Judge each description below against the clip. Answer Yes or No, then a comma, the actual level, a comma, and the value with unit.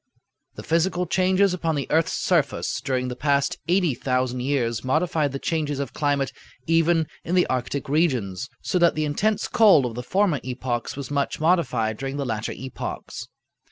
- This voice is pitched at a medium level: Yes, medium, 145 Hz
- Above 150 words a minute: Yes, average, 165 wpm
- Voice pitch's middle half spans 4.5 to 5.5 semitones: Yes, average, 4.9 semitones